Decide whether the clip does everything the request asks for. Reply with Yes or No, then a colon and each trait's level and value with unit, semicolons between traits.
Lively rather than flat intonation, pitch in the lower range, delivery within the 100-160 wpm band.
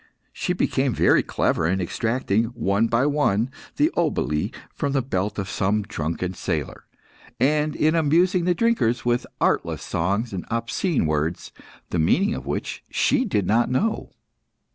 Yes: wide, 7.6 semitones; low, 115 Hz; average, 150 wpm